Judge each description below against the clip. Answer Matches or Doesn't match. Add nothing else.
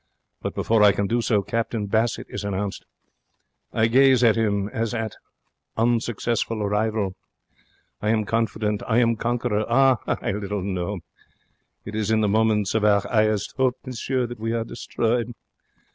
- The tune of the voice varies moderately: Doesn't match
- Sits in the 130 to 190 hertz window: Doesn't match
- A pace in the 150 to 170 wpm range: Matches